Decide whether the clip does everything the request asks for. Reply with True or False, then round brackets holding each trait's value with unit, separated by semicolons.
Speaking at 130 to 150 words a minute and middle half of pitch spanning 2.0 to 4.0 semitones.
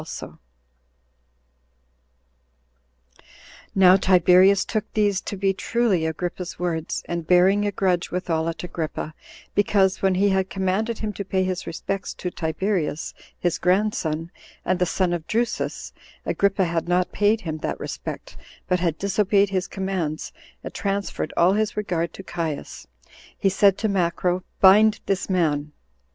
True (140 wpm; 2.6 semitones)